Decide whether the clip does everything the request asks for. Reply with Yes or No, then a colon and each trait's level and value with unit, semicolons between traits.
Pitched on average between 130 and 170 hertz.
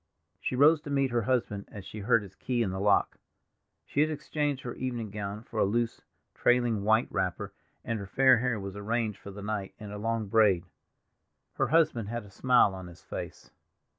No: low, 110 Hz